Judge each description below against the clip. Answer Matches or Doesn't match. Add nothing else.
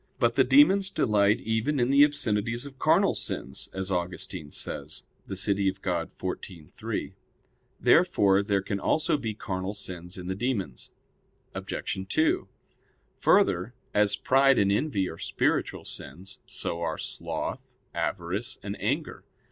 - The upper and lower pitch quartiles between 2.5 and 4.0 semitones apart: Doesn't match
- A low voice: Matches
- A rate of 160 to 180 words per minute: Doesn't match